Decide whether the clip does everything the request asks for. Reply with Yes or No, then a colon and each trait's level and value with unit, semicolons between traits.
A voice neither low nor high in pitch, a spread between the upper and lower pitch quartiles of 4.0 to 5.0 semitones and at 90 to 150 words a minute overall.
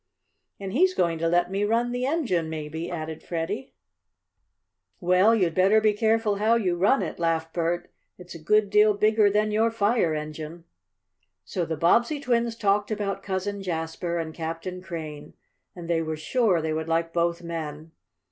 No: medium, 180 Hz; average, 4.5 semitones; average, 170 wpm